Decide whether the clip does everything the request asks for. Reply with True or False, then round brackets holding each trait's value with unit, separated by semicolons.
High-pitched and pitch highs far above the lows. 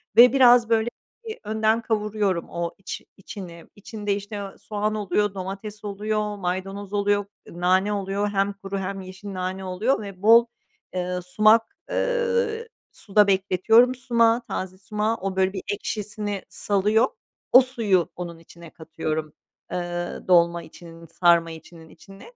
False (200 Hz; 2.8 semitones)